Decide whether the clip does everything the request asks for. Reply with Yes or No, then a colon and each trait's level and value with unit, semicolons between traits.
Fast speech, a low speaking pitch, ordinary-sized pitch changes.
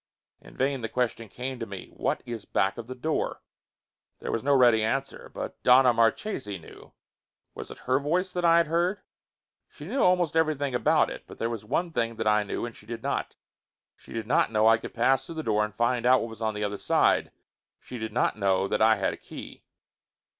Yes: fast, 225 wpm; low, 120 Hz; average, 4.0 semitones